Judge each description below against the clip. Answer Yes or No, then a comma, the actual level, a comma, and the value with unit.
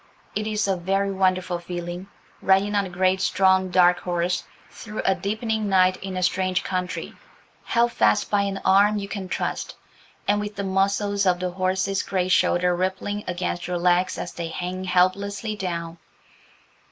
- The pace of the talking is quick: No, average, 165 wpm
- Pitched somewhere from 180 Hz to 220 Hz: Yes, high, 190 Hz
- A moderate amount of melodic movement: No, narrow, 1.8 semitones